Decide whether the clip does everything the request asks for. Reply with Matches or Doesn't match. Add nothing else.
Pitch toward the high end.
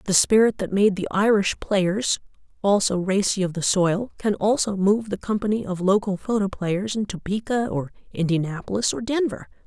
Matches